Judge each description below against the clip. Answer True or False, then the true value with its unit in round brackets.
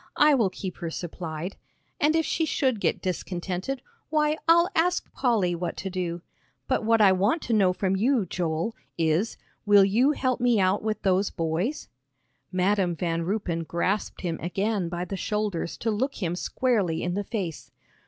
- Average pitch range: True (4.8 semitones)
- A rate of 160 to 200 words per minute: True (175 wpm)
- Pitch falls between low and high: False (195 Hz)